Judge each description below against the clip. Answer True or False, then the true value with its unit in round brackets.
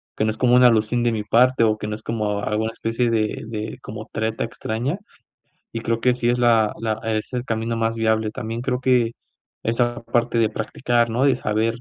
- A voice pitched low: True (115 Hz)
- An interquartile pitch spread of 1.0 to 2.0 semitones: True (1.7 semitones)